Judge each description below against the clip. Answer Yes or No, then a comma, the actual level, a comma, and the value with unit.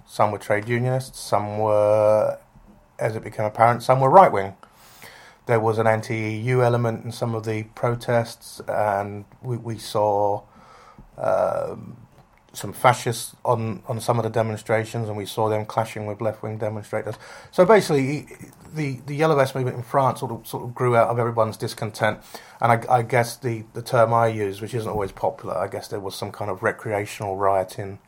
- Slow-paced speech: No, average, 185 wpm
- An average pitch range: No, narrow, 2.3 semitones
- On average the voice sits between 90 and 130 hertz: Yes, low, 115 Hz